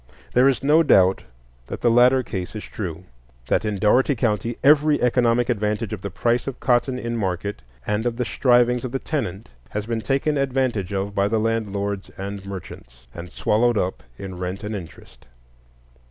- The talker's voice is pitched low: Yes, low, 110 Hz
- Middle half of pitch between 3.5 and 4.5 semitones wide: Yes, average, 3.8 semitones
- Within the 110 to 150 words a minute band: No, average, 180 wpm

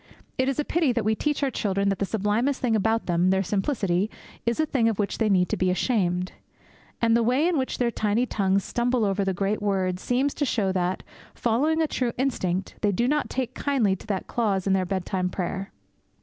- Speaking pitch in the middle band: No, high, 215 Hz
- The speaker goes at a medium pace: No, fast, 220 wpm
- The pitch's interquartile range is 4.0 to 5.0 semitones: Yes, average, 4.7 semitones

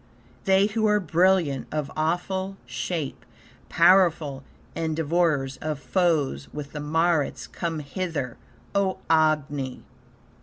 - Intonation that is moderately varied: Yes, average, 3.9 semitones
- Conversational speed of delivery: No, slow, 110 wpm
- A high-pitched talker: No, medium, 160 Hz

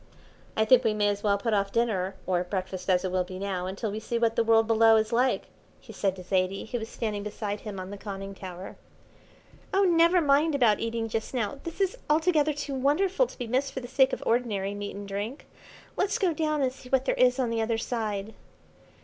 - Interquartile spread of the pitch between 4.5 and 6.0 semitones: Yes, average, 4.8 semitones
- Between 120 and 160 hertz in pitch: No, high, 225 Hz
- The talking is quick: Yes, fast, 230 wpm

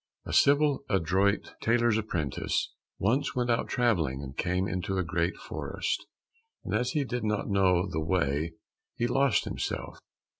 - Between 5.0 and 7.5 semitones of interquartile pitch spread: Yes, wide, 5.6 semitones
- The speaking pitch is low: Yes, low, 100 Hz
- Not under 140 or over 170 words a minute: Yes, average, 150 wpm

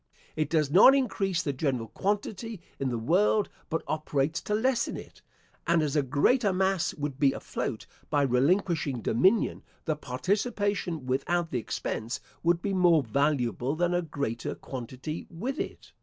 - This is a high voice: No, medium, 160 Hz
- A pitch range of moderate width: No, wide, 5.9 semitones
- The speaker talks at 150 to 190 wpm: Yes, average, 155 wpm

